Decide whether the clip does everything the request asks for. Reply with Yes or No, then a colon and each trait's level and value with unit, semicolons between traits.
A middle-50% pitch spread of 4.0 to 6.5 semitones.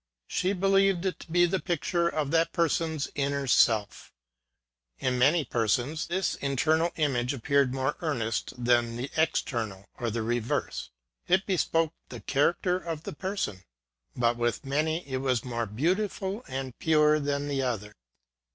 Yes: wide, 5.6 semitones